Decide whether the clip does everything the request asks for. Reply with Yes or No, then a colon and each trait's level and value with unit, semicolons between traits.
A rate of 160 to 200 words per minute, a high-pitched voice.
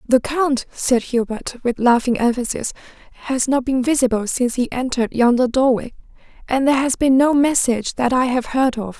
Yes: average, 180 wpm; very high, 255 Hz